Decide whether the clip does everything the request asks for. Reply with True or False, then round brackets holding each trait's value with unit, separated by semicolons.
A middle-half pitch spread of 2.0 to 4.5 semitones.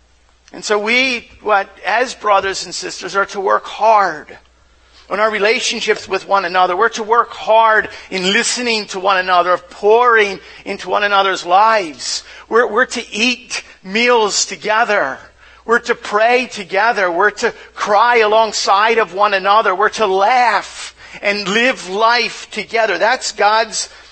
True (2.6 semitones)